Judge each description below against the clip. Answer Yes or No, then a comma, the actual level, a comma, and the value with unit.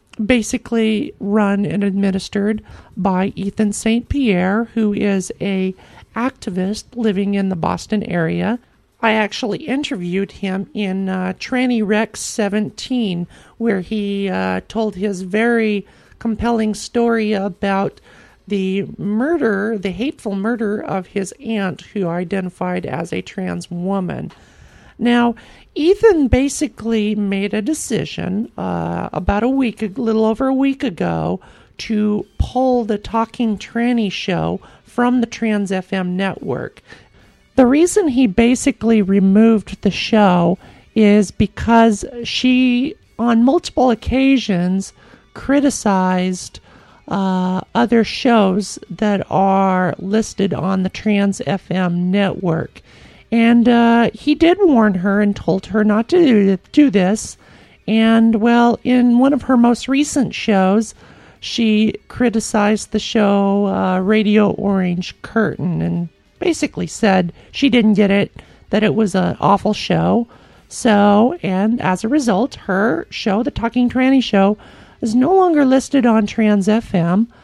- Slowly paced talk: Yes, slow, 125 wpm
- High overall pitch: Yes, high, 215 Hz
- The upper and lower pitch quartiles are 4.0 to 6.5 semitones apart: No, average, 3.3 semitones